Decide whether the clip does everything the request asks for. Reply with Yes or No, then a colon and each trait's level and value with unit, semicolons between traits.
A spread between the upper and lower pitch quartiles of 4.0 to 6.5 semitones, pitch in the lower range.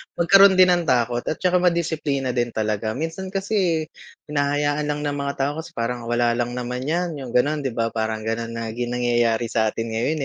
Yes: average, 5.3 semitones; low, 130 Hz